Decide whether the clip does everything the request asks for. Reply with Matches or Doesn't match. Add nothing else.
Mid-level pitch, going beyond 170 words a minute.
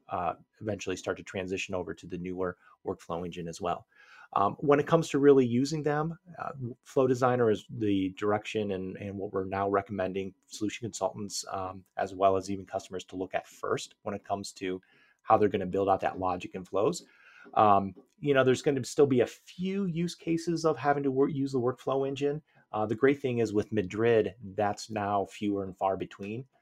Doesn't match